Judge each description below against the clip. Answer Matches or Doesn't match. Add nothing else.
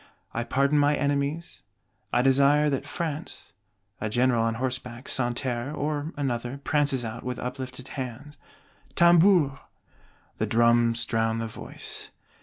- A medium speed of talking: Doesn't match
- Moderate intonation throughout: Matches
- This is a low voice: Matches